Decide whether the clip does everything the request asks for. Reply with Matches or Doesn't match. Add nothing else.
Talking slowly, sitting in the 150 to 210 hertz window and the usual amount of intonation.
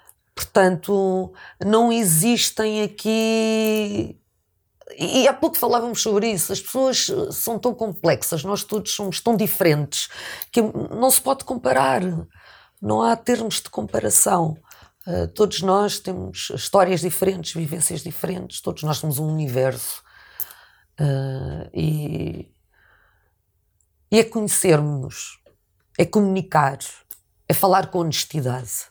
Doesn't match